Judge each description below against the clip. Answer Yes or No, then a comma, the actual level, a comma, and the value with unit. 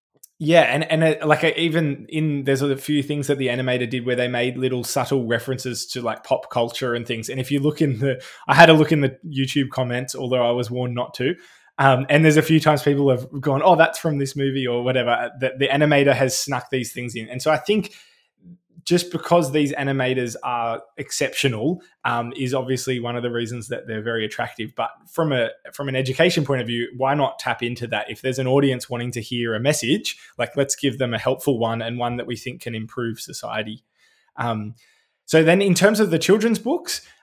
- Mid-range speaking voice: No, low, 130 Hz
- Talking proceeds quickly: Yes, fast, 220 wpm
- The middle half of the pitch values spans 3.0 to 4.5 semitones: Yes, average, 3.7 semitones